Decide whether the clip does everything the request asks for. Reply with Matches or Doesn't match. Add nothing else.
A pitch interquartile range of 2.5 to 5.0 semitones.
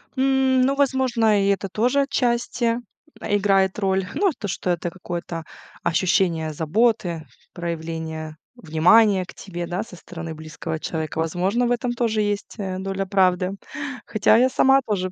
Doesn't match